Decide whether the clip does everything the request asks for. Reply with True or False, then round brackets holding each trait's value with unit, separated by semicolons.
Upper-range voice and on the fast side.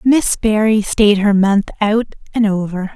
False (210 Hz; 160 wpm)